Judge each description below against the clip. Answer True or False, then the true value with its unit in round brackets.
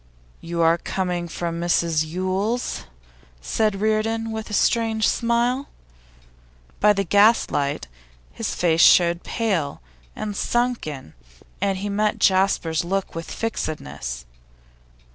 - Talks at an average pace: False (110 wpm)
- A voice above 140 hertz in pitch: True (190 Hz)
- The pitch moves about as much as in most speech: True (4.7 semitones)